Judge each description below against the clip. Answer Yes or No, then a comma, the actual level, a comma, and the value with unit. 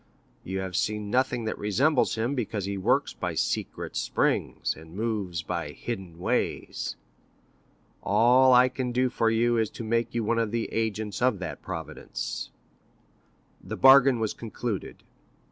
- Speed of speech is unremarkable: Yes, average, 150 wpm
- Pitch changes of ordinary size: Yes, average, 3.5 semitones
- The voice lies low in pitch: Yes, low, 110 Hz